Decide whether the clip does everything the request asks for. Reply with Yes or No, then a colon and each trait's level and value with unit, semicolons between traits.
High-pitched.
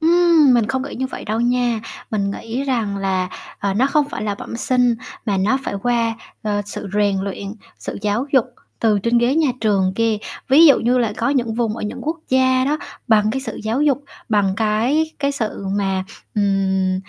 Yes: high, 230 Hz